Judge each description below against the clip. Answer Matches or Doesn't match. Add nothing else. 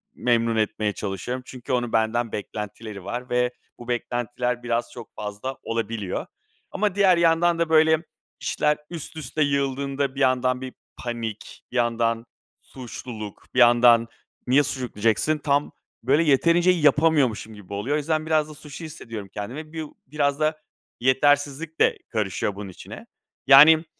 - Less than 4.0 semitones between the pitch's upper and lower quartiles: Doesn't match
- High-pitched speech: Doesn't match